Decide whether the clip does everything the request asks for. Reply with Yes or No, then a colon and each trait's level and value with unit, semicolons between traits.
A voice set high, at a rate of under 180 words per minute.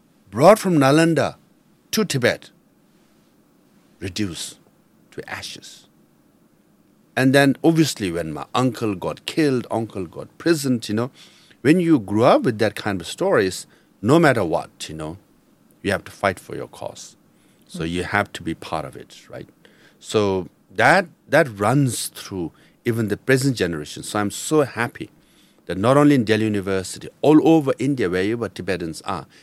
No: low, 120 Hz; average, 160 wpm